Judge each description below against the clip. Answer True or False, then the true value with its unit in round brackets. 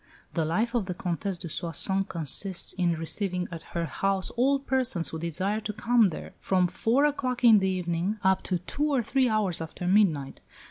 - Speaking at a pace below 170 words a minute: False (190 wpm)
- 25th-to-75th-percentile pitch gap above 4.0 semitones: True (4.7 semitones)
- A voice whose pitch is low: False (190 Hz)